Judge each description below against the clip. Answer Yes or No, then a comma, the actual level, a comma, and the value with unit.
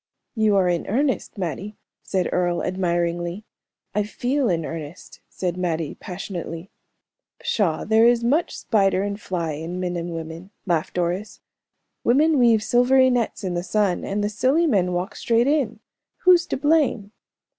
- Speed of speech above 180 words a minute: No, average, 155 wpm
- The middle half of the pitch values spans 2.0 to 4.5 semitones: No, average, 5.3 semitones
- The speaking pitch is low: No, high, 195 Hz